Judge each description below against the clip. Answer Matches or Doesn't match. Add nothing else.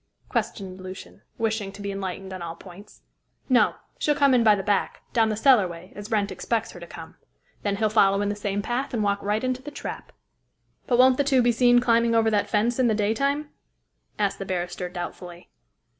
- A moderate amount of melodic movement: Matches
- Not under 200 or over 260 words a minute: Matches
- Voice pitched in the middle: Doesn't match